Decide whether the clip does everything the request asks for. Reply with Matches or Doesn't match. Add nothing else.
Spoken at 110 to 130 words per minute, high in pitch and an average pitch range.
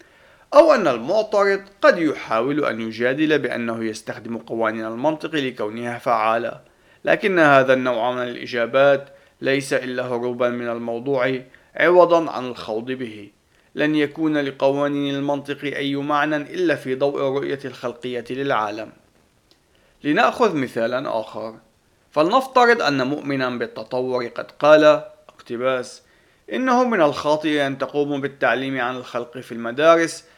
Doesn't match